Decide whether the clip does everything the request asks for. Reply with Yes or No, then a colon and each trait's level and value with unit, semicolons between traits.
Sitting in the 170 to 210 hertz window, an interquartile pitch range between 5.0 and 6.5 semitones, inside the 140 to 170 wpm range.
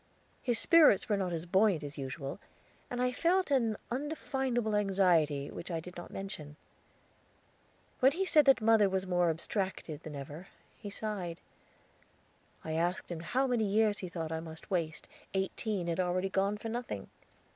Yes: high, 190 Hz; average, 5.3 semitones; average, 165 wpm